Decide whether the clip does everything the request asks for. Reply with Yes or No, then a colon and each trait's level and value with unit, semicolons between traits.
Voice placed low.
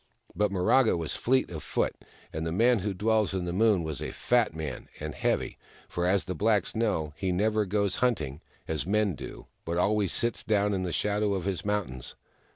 Yes: low, 100 Hz